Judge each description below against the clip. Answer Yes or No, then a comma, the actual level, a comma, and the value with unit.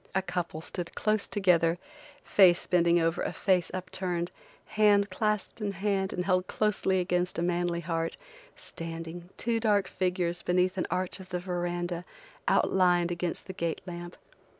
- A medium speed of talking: Yes, average, 155 wpm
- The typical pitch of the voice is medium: Yes, medium, 180 Hz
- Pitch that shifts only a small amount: Yes, narrow, 1.7 semitones